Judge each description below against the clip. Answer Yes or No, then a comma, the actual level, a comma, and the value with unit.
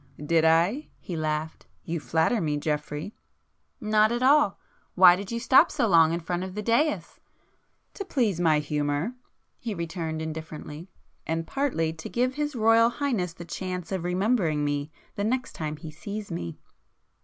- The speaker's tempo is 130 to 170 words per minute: Yes, average, 160 wpm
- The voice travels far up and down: Yes, wide, 6.1 semitones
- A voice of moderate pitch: Yes, medium, 175 Hz